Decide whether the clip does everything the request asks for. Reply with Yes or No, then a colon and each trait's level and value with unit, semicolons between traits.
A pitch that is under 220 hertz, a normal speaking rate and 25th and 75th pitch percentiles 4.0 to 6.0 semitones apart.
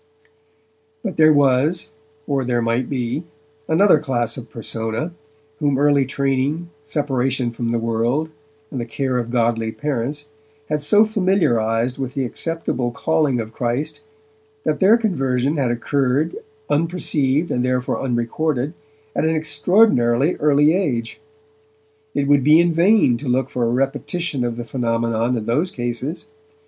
Yes: low, 135 Hz; average, 145 wpm; average, 4.4 semitones